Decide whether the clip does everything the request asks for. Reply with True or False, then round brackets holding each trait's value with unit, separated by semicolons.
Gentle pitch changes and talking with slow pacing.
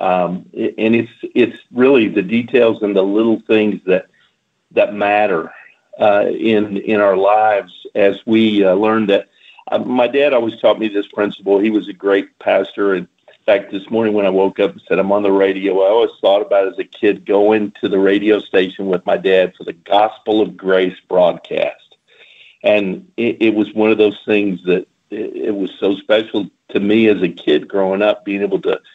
False (2.2 semitones; 200 wpm)